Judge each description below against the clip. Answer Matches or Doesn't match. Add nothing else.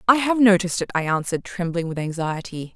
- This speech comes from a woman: Matches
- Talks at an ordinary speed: Matches